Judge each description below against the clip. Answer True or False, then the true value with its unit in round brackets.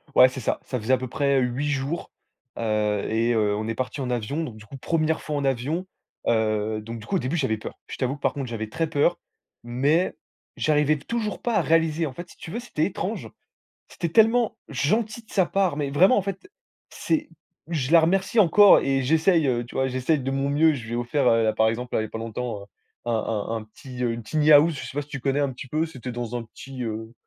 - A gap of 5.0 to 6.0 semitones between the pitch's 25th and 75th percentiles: True (5.4 semitones)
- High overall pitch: False (135 Hz)